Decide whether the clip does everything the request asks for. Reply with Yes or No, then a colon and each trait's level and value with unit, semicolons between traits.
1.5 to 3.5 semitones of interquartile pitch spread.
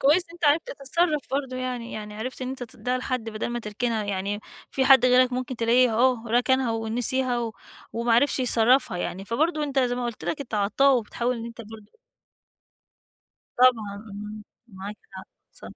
Yes: average, 2.9 semitones